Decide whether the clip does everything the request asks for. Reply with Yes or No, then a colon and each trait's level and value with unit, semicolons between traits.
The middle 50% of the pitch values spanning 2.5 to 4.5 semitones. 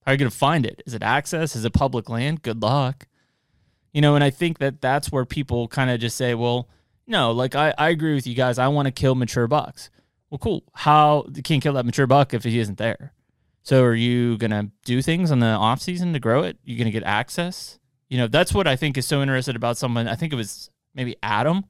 Yes: average, 3.5 semitones